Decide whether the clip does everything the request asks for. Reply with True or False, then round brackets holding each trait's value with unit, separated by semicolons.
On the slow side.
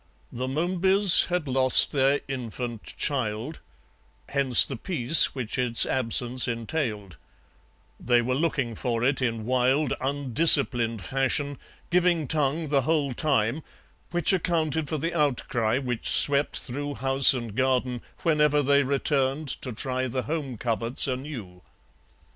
True (130 wpm)